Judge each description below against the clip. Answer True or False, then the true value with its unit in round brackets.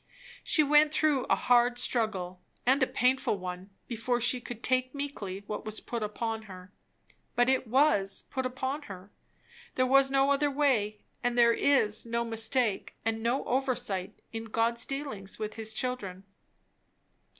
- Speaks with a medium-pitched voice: False (240 Hz)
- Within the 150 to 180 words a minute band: True (155 wpm)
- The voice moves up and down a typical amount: True (3.7 semitones)